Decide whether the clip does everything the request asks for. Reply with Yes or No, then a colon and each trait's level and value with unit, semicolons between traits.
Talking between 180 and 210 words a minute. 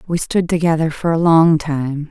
Yes: average, 200 wpm